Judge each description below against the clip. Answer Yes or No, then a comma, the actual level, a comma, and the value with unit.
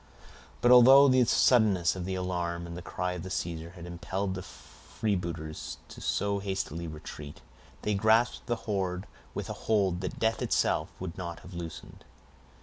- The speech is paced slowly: No, average, 165 wpm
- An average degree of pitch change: Yes, average, 3.3 semitones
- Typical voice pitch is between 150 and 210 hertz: No, very low, 90 Hz